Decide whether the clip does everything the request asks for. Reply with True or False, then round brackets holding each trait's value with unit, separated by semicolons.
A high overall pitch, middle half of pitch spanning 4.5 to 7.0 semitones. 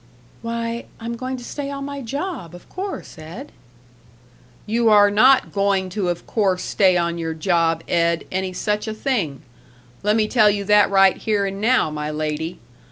True (205 Hz; 5.1 semitones)